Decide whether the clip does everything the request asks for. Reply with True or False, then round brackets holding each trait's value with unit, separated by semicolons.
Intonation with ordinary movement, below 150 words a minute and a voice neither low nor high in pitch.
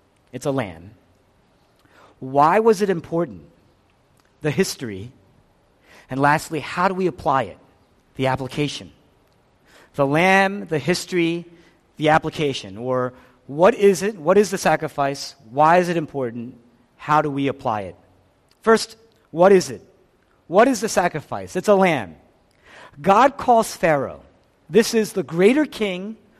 False (7.4 semitones; 135 wpm; 150 Hz)